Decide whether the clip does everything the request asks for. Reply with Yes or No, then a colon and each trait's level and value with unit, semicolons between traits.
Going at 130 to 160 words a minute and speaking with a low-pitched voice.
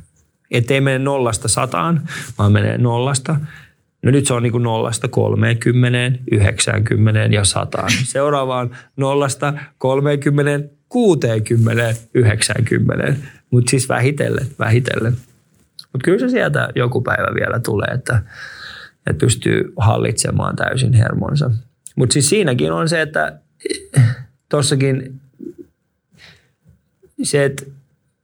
No: average, 105 wpm; low, 130 Hz